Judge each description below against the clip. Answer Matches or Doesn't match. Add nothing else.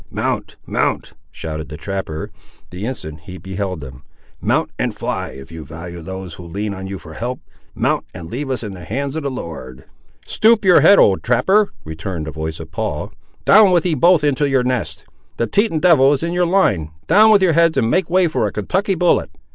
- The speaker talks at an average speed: Doesn't match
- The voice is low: Matches